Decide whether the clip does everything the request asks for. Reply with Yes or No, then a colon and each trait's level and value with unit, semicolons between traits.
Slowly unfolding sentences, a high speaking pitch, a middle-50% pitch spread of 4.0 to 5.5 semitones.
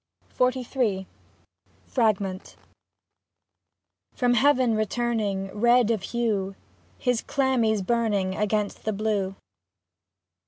No: slow, 85 wpm; high, 220 Hz; average, 3.5 semitones